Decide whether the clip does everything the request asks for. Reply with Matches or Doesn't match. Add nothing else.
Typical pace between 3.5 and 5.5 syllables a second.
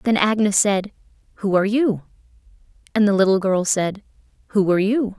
Doesn't match